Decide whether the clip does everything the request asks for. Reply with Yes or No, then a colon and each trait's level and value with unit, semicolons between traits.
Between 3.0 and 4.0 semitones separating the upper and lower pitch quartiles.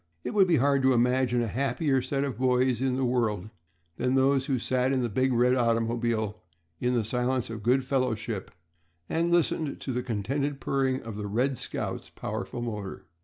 No: narrow, 2.4 semitones